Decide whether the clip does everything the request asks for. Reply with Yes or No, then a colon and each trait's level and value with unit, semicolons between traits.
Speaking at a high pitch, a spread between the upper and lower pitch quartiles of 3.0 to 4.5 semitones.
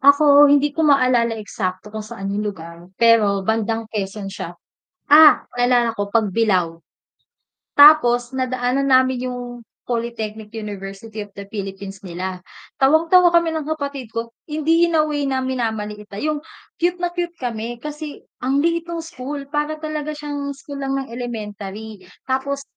No: high, 245 Hz; wide, 5.6 semitones